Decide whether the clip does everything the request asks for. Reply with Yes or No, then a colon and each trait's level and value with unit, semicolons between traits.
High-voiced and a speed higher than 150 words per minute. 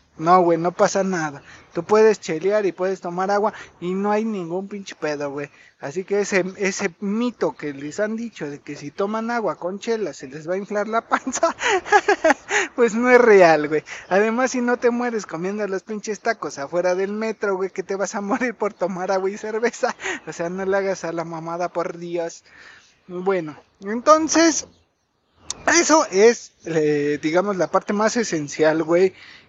Yes: high, 195 Hz; average, 185 wpm